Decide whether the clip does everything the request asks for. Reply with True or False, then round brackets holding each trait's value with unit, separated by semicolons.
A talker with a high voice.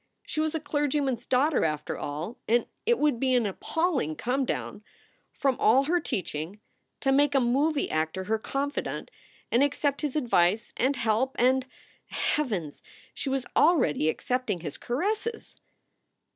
True (260 Hz)